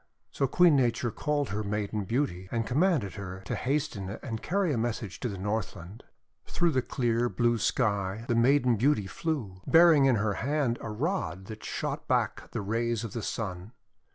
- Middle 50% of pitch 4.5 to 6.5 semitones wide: Yes, average, 5.2 semitones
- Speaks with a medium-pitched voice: No, low, 115 Hz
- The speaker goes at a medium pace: Yes, average, 180 wpm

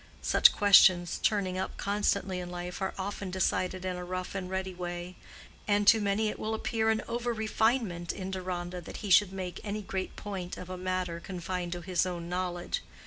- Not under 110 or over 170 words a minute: No, average, 195 wpm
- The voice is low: No, medium, 185 Hz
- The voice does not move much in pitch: Yes, narrow, 2.2 semitones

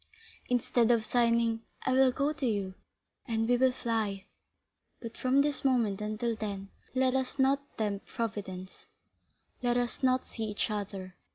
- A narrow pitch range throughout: No, average, 3.4 semitones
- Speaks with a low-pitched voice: No, high, 230 Hz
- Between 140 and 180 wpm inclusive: Yes, average, 155 wpm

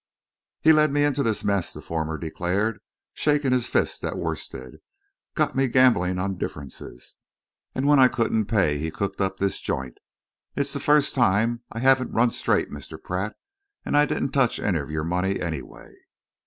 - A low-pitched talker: Yes, low, 110 Hz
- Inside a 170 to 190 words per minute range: Yes, average, 175 wpm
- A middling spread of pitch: No, wide, 7.0 semitones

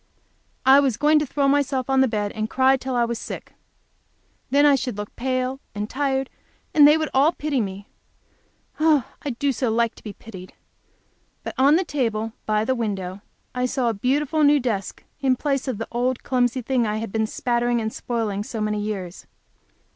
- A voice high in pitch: Yes, very high, 250 Hz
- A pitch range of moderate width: Yes, average, 4.0 semitones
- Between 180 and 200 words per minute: Yes, average, 190 wpm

